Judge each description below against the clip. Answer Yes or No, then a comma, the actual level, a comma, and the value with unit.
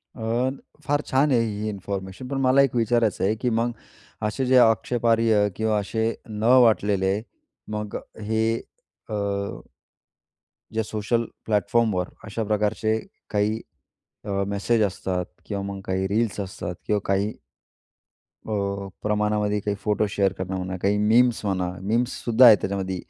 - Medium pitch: No, low, 105 Hz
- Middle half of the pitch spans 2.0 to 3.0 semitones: Yes, narrow, 2.5 semitones